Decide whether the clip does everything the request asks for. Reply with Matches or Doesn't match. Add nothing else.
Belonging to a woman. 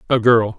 Doesn't match